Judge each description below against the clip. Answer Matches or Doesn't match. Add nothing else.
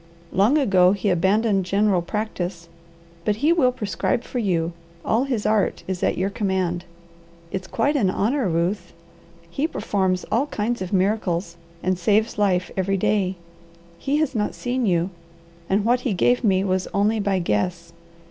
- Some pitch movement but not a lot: Matches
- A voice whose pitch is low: Doesn't match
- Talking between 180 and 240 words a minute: Doesn't match